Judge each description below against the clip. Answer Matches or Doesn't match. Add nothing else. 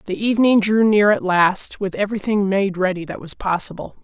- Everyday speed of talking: Matches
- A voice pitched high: Matches